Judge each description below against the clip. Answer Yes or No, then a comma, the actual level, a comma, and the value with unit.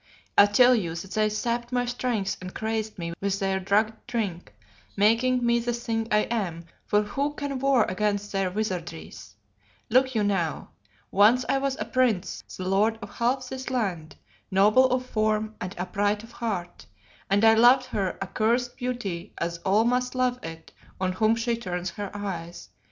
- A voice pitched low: No, high, 215 Hz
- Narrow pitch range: No, average, 4.1 semitones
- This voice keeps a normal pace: Yes, average, 175 wpm